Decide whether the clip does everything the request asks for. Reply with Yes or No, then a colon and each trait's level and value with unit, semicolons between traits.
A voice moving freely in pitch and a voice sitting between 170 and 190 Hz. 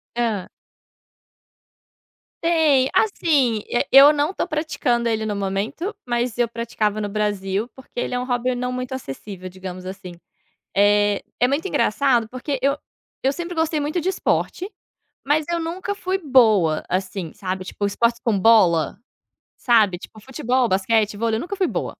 No: wide, 5.9 semitones; high, 235 Hz